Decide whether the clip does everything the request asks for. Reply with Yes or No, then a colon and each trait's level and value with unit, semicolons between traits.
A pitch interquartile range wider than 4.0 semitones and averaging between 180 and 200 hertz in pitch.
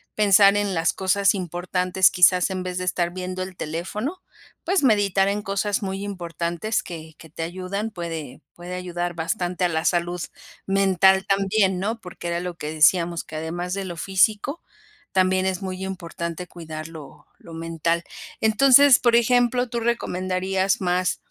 No: narrow, 2.5 semitones; medium, 185 Hz